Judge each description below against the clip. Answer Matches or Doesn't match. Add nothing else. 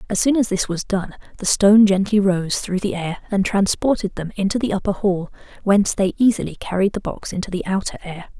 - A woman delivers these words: Matches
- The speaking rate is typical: Doesn't match